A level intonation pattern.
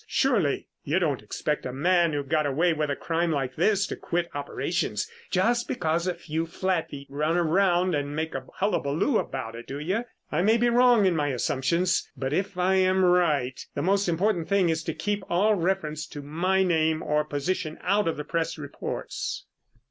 No: average, 4.2 semitones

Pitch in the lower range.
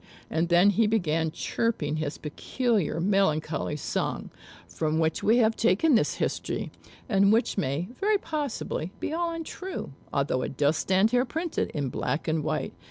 No: high, 190 Hz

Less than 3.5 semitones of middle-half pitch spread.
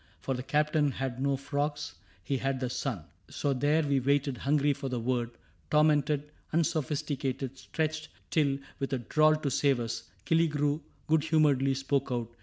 Yes: narrow, 2.4 semitones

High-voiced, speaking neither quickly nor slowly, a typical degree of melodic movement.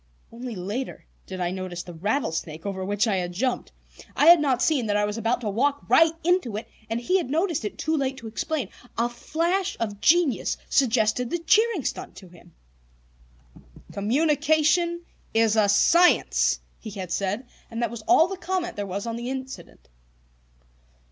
No: high, 240 Hz; average, 175 wpm; wide, 7.4 semitones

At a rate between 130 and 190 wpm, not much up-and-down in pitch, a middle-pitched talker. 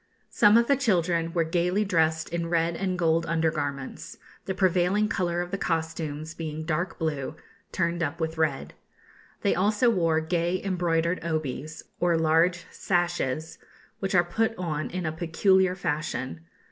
Yes: average, 155 wpm; narrow, 2.2 semitones; medium, 170 Hz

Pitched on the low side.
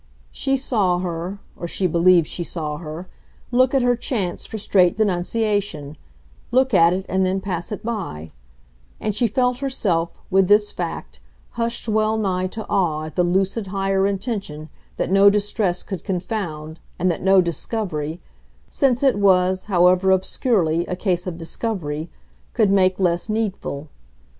No: high, 190 Hz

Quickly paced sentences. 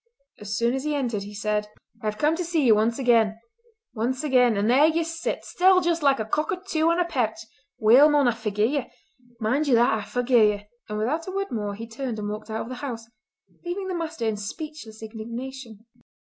Yes: fast, 210 wpm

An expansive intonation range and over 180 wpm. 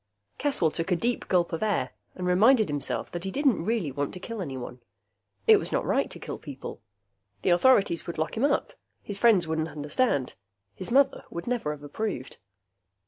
Yes: wide, 6.6 semitones; average, 190 wpm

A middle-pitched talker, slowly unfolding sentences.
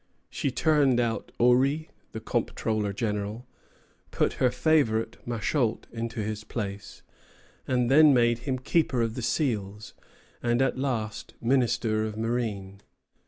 No: low, 120 Hz; slow, 120 wpm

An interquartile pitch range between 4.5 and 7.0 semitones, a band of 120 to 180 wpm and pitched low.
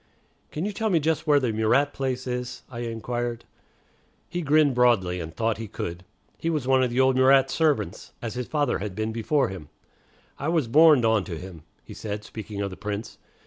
No: average, 5.1 semitones; fast, 205 wpm; low, 120 Hz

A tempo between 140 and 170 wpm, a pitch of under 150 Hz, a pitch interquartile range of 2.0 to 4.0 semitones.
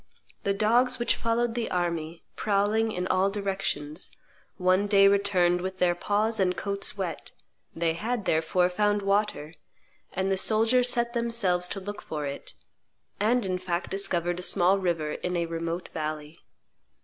No: average, 155 wpm; high, 190 Hz; average, 3.2 semitones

